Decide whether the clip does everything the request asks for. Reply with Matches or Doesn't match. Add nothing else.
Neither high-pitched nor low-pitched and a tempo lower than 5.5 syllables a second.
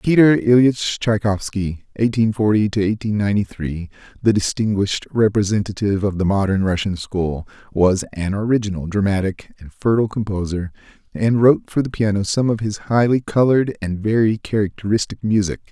Doesn't match